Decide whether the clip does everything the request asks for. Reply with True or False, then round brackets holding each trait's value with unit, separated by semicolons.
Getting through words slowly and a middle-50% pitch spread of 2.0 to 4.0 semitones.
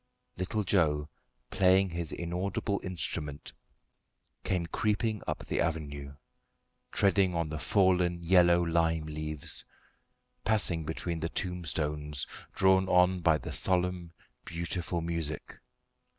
True (105 wpm; 2.8 semitones)